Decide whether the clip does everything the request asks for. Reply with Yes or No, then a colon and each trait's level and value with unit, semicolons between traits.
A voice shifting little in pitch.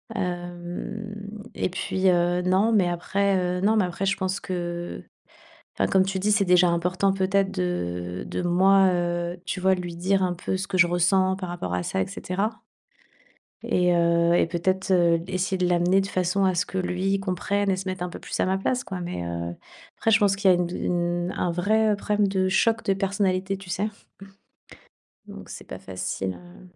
Yes: narrow, 1.9 semitones